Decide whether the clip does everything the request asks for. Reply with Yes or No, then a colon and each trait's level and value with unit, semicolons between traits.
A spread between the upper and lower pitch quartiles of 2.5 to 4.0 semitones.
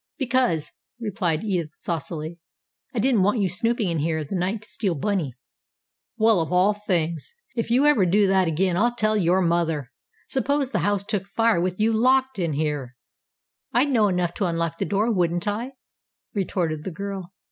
No: average, 4.6 semitones